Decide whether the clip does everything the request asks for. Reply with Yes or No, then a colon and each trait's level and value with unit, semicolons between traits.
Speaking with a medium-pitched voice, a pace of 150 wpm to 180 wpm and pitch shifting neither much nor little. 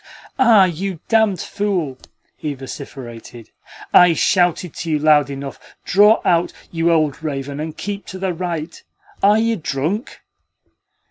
No: medium, 165 Hz; slow, 135 wpm; average, 5.0 semitones